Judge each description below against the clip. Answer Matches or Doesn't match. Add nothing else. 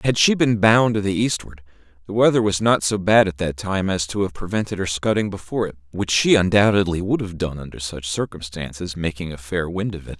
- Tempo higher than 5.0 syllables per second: Matches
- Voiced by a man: Matches